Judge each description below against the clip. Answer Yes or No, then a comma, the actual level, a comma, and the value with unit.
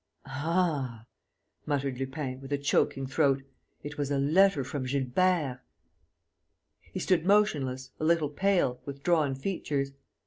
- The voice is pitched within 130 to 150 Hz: Yes, medium, 140 Hz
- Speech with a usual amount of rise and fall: Yes, average, 3.7 semitones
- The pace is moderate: No, slow, 130 wpm